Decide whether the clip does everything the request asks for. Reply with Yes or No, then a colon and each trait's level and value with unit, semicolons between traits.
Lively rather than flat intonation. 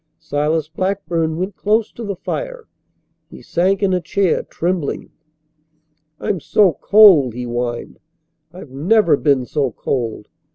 Yes: wide, 5.7 semitones